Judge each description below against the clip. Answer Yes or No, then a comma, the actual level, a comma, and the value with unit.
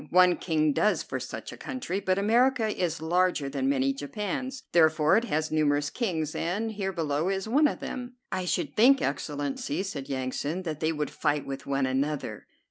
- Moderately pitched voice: Yes, medium, 165 Hz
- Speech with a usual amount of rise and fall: No, wide, 5.8 semitones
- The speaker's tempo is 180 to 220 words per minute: Yes, average, 190 wpm